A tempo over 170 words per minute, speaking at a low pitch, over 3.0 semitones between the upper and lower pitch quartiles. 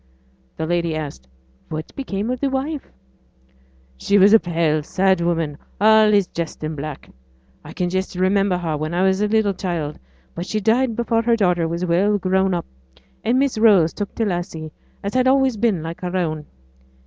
No: average, 185 wpm; medium, 185 Hz; average, 4.4 semitones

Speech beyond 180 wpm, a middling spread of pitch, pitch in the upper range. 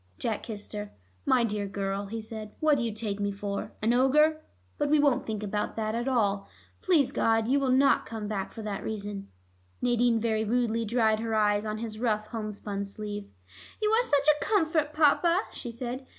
Yes: average, 195 wpm; average, 4.0 semitones; high, 225 Hz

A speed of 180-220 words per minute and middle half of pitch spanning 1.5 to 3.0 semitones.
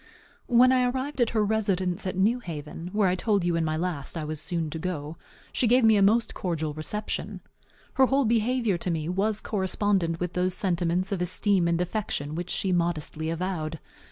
No: average, 195 wpm; average, 4.4 semitones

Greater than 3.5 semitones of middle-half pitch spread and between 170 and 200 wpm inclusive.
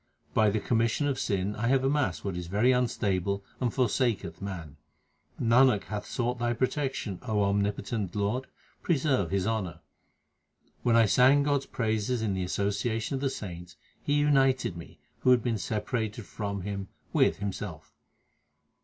No: average, 4.2 semitones; average, 155 wpm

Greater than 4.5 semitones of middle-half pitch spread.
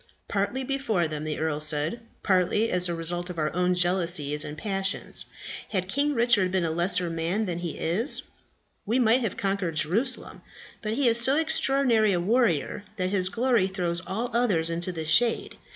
Yes: average, 5.2 semitones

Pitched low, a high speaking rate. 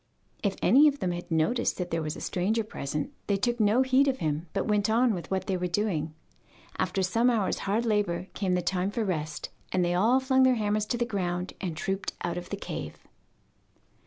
No: high, 195 Hz; fast, 220 wpm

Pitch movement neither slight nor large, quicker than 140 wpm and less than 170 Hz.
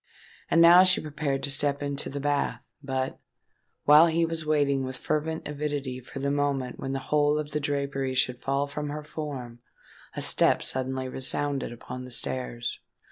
No: narrow, 2.1 semitones; average, 175 wpm; medium, 140 Hz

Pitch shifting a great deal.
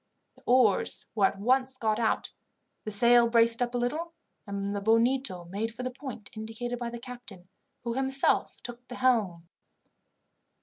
No: average, 2.7 semitones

